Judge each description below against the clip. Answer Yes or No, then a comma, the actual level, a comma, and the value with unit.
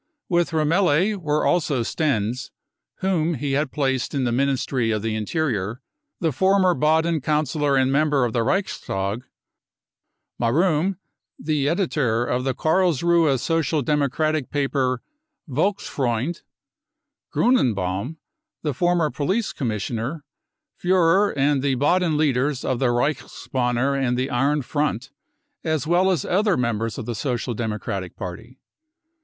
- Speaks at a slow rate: Yes, slow, 125 wpm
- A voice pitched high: No, medium, 140 Hz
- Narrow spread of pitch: No, average, 4.8 semitones